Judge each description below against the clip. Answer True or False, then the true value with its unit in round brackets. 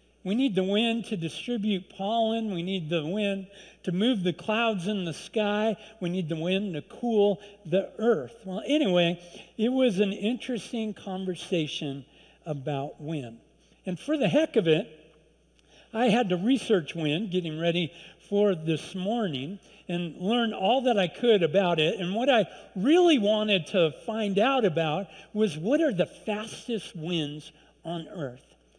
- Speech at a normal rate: True (160 wpm)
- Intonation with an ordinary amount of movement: True (4.7 semitones)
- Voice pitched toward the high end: True (195 Hz)